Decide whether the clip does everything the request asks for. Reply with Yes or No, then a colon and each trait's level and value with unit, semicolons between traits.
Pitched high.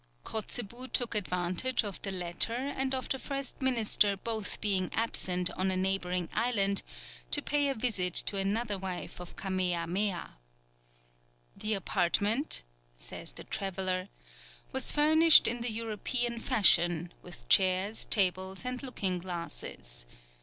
Yes: high, 200 Hz